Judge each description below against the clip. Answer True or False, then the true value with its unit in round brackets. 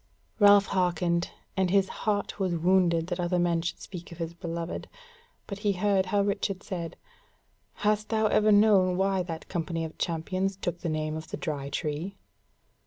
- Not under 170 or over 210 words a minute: True (175 wpm)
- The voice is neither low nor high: True (180 Hz)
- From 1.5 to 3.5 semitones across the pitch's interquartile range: True (2.9 semitones)